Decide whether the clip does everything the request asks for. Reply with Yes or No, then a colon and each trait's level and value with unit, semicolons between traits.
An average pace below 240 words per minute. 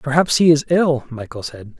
Yes: average, 200 wpm